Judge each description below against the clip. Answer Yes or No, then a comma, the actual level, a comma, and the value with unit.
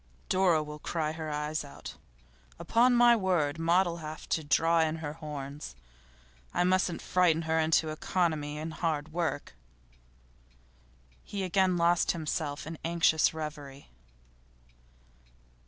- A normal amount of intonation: No, narrow, 2.3 semitones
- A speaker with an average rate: No, slow, 125 wpm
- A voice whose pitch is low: No, medium, 160 Hz